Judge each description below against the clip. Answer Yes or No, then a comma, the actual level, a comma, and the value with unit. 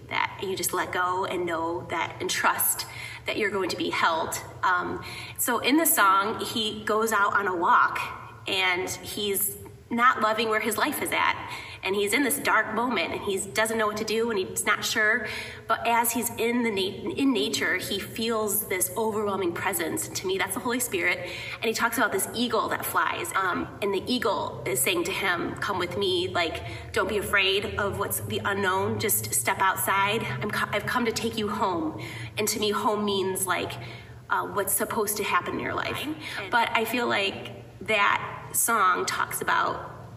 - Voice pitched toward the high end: Yes, high, 215 Hz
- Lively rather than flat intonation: No, average, 3.3 semitones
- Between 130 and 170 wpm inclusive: No, average, 200 wpm